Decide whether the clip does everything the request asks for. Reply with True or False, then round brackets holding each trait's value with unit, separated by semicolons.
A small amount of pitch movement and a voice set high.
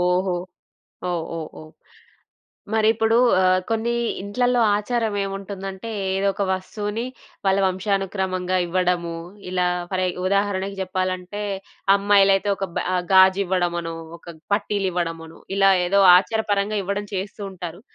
True (2.0 semitones; 195 Hz)